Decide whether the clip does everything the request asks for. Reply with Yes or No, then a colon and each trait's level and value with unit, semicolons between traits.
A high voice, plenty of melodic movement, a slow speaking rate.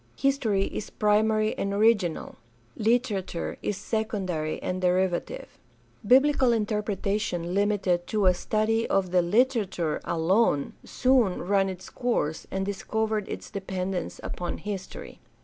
No: high, 200 Hz; average, 3.1 semitones; slow, 115 wpm